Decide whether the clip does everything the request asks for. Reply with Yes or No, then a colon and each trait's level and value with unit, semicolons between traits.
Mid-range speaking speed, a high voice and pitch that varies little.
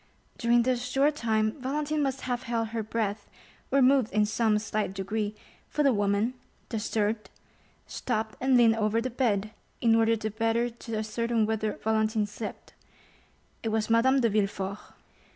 Yes: average, 155 wpm; high, 225 Hz; narrow, 2.2 semitones